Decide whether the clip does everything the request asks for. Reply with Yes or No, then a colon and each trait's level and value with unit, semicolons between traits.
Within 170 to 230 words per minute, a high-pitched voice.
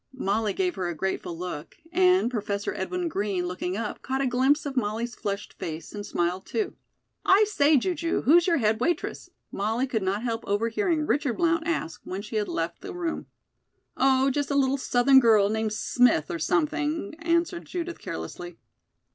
Yes: average, 180 wpm; high, 245 Hz